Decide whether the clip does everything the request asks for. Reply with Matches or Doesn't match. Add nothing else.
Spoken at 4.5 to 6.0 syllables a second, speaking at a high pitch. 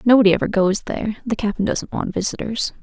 Doesn't match